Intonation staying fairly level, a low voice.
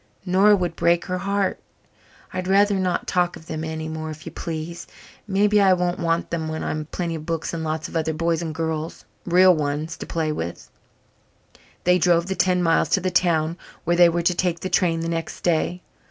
No: narrow, 2.3 semitones; medium, 170 Hz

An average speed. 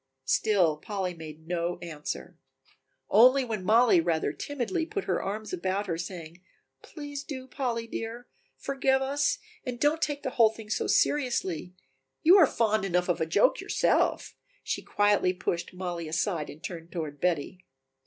Yes: average, 155 wpm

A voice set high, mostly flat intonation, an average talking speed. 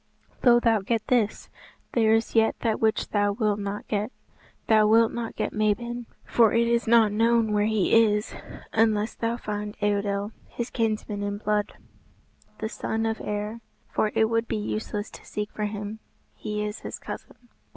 Yes: high, 215 Hz; narrow, 1.6 semitones; average, 170 wpm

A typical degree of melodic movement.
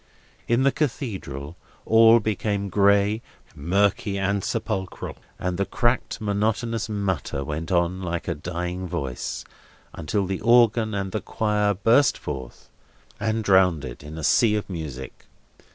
Yes: average, 4.1 semitones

